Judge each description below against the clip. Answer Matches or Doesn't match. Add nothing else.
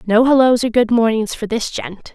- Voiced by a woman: Matches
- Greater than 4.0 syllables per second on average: Matches